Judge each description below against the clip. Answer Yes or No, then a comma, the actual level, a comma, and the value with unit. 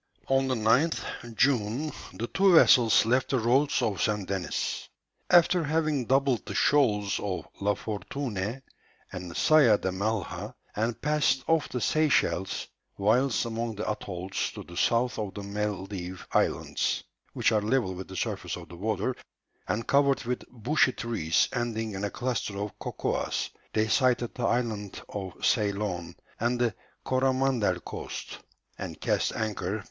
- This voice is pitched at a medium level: No, low, 110 Hz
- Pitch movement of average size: Yes, average, 4.4 semitones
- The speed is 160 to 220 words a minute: No, average, 150 wpm